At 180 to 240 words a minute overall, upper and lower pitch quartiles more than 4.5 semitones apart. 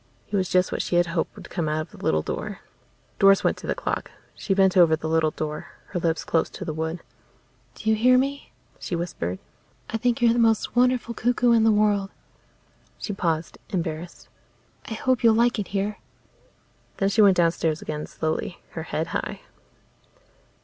Yes: average, 190 wpm; wide, 5.5 semitones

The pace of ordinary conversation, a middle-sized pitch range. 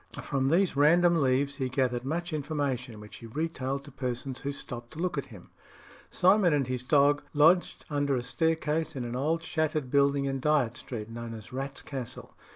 Yes: average, 185 wpm; average, 3.5 semitones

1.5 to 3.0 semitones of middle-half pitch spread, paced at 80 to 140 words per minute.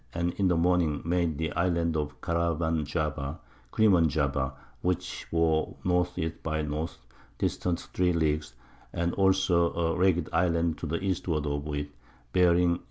No: narrow, 2.4 semitones; average, 155 wpm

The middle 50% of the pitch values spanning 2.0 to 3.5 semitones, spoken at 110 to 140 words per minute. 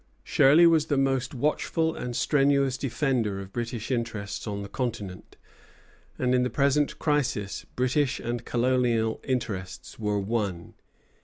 No: average, 4.2 semitones; slow, 135 wpm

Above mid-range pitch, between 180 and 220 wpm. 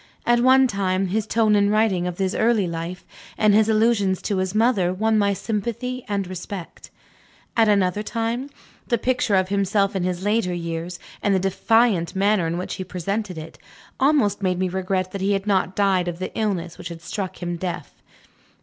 Yes: high, 195 Hz; average, 190 wpm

